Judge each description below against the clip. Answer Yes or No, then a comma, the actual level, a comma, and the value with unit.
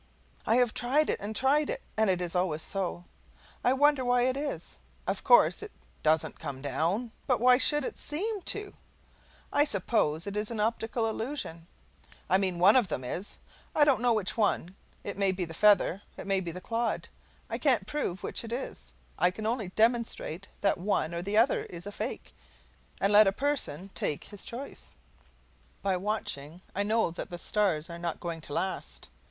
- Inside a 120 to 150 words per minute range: No, average, 190 wpm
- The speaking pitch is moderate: No, high, 205 Hz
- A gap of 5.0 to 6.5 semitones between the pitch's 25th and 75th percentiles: Yes, wide, 5.5 semitones